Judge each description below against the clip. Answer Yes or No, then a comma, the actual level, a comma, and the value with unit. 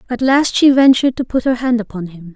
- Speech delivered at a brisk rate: Yes, fast, 255 wpm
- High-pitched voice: Yes, high, 240 Hz